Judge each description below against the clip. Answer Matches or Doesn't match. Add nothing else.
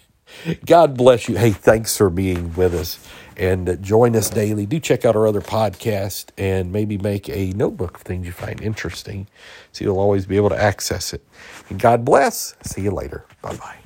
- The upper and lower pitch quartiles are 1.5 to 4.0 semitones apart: Matches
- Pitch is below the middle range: Matches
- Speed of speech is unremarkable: Matches